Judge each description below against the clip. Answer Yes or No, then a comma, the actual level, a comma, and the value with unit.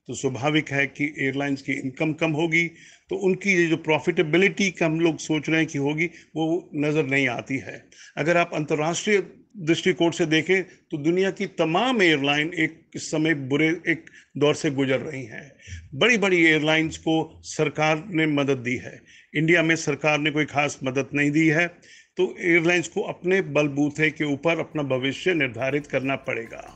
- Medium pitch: Yes, medium, 155 Hz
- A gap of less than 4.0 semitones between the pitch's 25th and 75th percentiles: Yes, average, 3.0 semitones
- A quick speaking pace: No, average, 170 wpm